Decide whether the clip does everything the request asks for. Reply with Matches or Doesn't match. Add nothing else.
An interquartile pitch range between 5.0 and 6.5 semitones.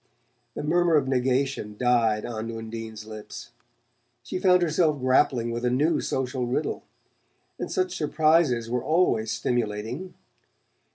Matches